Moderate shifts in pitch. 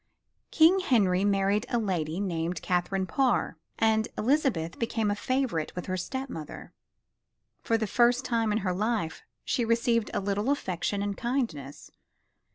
Yes: average, 4.6 semitones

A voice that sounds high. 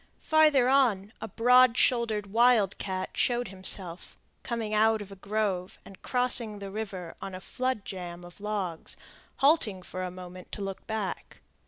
Yes: high, 210 Hz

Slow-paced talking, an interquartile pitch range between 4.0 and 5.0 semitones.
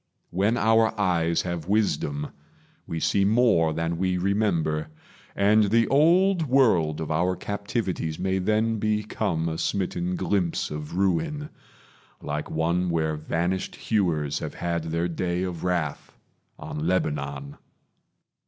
Yes: slow, 125 wpm; average, 4.6 semitones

